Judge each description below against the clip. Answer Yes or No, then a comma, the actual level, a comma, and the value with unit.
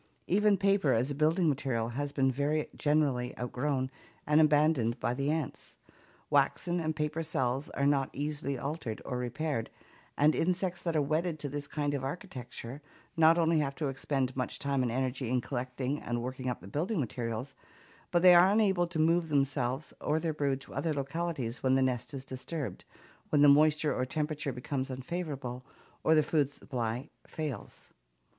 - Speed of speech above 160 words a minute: Yes, average, 175 wpm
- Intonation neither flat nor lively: Yes, average, 3.4 semitones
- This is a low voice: No, medium, 145 Hz